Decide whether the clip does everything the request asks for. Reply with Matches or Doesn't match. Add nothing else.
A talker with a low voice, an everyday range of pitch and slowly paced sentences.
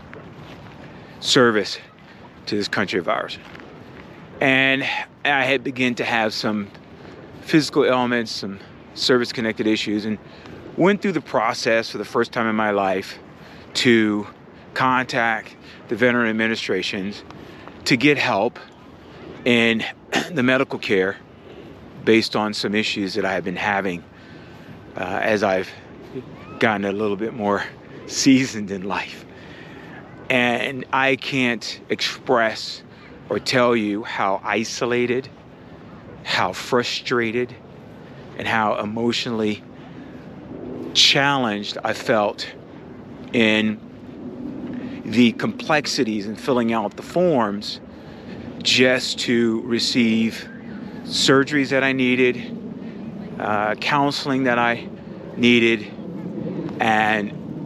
Matches